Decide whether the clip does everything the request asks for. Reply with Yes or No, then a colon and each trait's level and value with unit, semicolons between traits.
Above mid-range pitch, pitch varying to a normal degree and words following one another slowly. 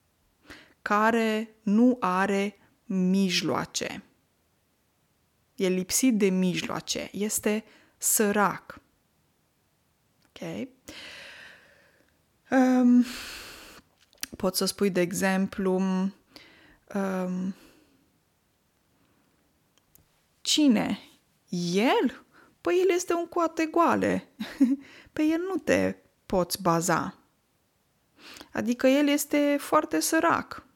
No: high, 220 Hz; wide, 7.1 semitones; slow, 75 wpm